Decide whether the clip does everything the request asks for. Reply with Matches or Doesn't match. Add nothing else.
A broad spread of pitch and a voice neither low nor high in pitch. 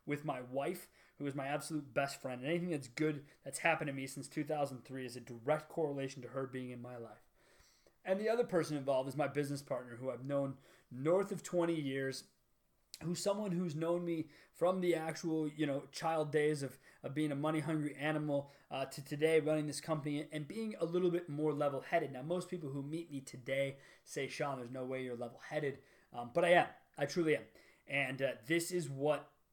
Doesn't match